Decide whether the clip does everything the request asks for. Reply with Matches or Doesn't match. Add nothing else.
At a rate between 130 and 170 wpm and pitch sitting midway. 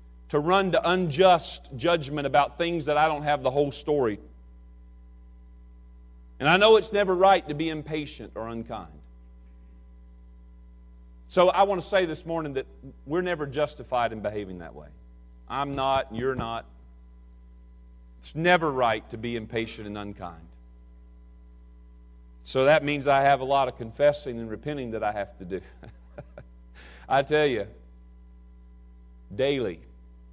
Doesn't match